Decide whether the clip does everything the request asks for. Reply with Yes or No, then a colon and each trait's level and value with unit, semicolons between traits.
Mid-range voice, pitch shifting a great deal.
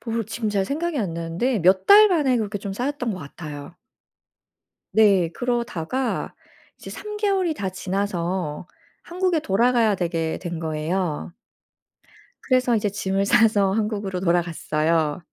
No: high, 200 Hz; wide, 6.0 semitones